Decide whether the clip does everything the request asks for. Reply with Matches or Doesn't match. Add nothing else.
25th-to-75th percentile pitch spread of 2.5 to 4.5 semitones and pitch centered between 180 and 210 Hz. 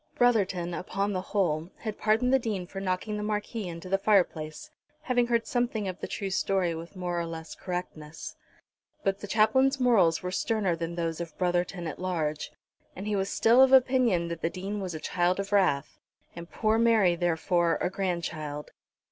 Matches